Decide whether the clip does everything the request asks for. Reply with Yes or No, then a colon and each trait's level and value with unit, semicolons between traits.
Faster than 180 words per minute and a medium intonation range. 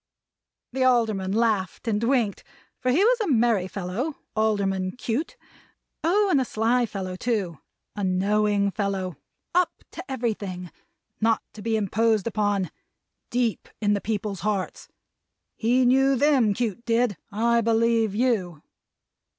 No: slow, 135 wpm; average, 3.6 semitones